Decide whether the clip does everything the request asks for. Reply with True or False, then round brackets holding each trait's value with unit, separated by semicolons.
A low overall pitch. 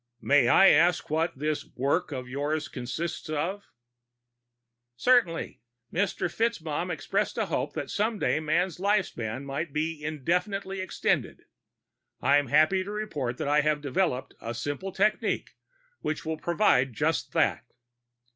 False (155 Hz)